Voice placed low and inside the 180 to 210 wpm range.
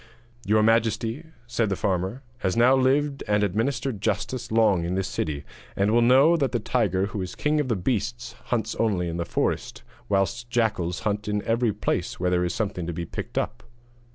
Yes: low, 110 Hz; average, 190 wpm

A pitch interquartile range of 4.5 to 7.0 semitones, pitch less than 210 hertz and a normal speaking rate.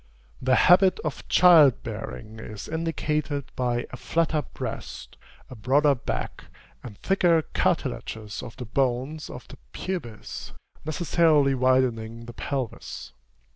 No: average, 5.0 semitones; low, 135 Hz; slow, 120 wpm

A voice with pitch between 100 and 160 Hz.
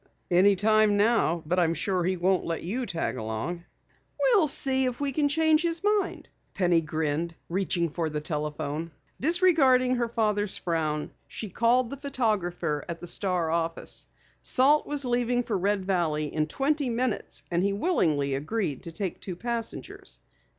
No: high, 195 Hz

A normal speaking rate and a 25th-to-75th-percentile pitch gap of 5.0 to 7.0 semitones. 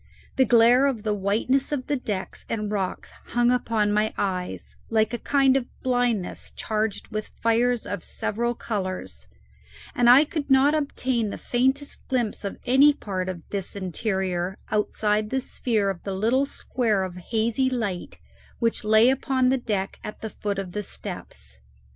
No: average, 165 wpm; average, 4.0 semitones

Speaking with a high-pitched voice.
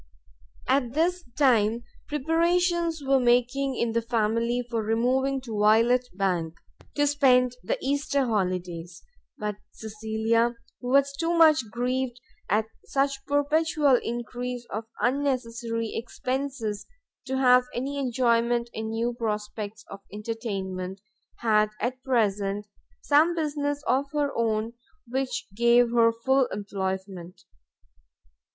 Yes: high, 240 Hz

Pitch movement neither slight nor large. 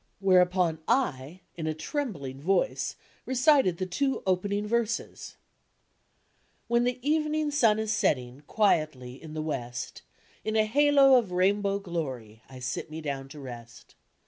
No: wide, 8.3 semitones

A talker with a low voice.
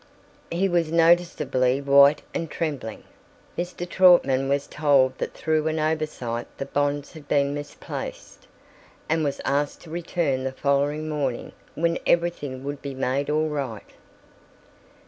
No: medium, 145 Hz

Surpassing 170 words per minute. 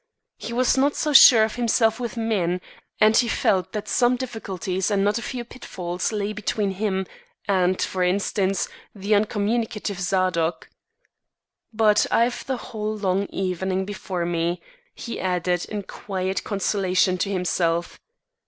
No: average, 145 wpm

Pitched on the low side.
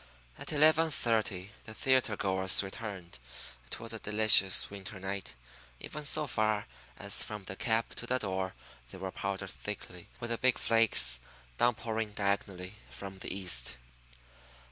Yes: low, 105 Hz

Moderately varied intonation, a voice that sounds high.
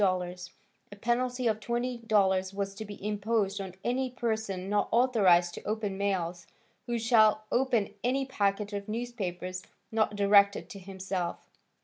Yes: average, 3.2 semitones; high, 205 Hz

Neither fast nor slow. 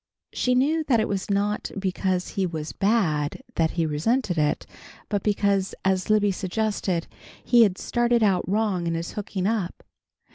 Yes: average, 160 wpm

